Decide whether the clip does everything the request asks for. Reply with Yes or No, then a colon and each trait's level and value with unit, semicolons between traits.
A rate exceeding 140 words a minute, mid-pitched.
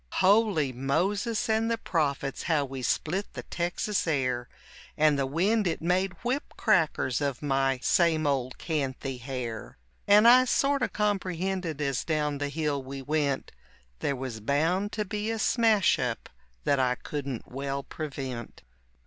Yes: average, 150 wpm; medium, 155 Hz